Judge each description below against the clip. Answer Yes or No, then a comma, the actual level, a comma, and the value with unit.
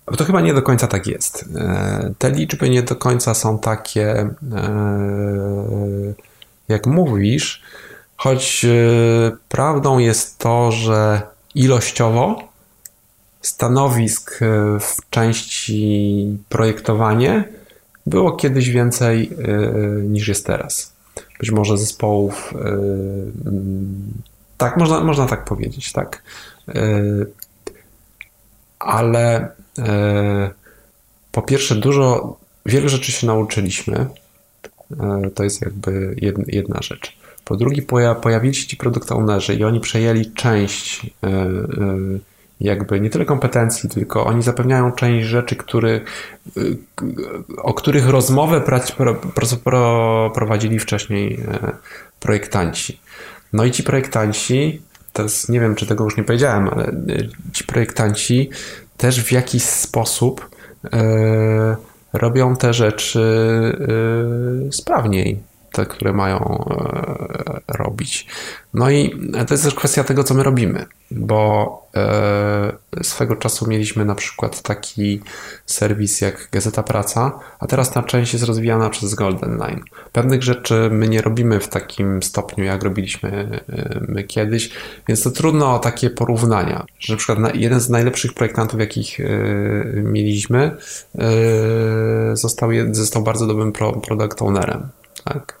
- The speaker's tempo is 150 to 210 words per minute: No, slow, 110 wpm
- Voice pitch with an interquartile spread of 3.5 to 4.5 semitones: No, average, 3.0 semitones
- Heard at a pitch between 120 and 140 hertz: No, low, 110 Hz